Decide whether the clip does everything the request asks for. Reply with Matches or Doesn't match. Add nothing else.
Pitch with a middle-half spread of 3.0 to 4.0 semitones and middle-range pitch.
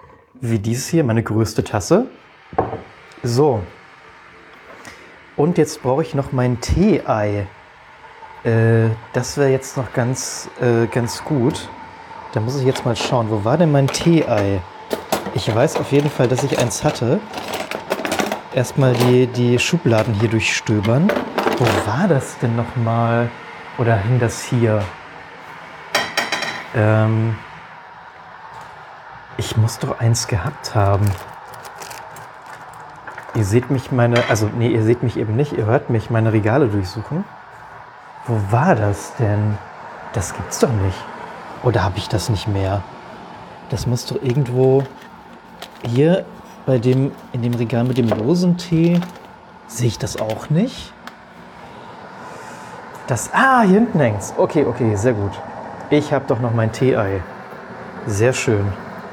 Doesn't match